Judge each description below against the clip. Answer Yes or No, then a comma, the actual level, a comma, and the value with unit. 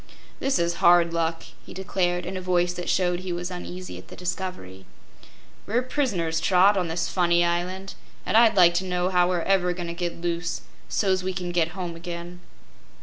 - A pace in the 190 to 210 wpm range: Yes, average, 195 wpm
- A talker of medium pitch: Yes, medium, 180 Hz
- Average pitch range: No, narrow, 1.4 semitones